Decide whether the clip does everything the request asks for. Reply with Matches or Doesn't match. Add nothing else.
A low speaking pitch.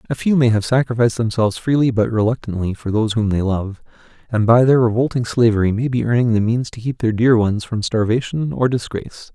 Matches